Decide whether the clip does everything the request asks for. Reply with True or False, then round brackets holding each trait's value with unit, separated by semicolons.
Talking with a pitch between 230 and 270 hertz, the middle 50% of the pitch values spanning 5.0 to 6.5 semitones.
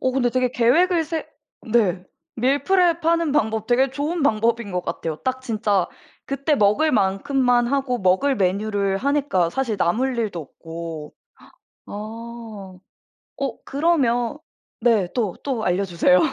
True (235 Hz; 5.6 semitones)